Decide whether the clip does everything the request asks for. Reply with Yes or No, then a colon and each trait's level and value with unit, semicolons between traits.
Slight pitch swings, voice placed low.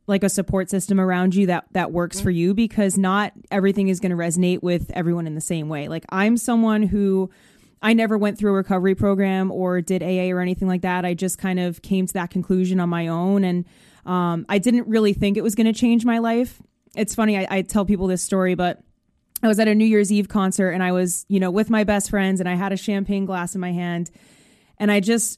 No: narrow, 2.3 semitones; high, 190 Hz